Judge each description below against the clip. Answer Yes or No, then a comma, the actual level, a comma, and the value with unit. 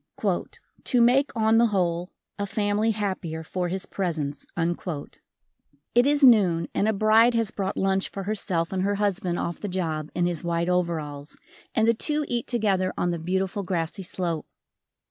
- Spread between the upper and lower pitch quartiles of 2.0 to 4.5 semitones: Yes, average, 4.0 semitones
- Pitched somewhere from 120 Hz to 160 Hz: No, high, 190 Hz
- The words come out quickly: No, average, 165 wpm